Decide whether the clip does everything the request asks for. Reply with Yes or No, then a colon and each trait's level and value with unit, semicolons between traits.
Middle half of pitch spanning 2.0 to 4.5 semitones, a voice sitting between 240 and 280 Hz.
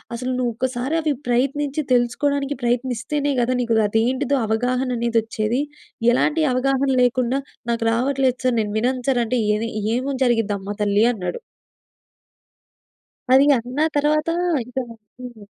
Yes: narrow, 2.5 semitones; very high, 250 Hz